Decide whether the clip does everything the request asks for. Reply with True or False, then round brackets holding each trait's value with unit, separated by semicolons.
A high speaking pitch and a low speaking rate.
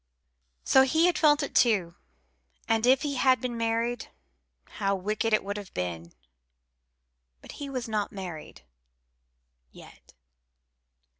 True (225 Hz; 130 wpm)